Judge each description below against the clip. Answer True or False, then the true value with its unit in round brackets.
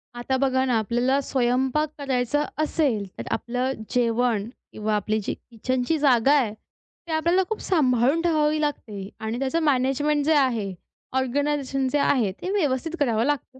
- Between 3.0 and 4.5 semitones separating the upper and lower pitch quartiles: True (3.5 semitones)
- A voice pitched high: True (260 Hz)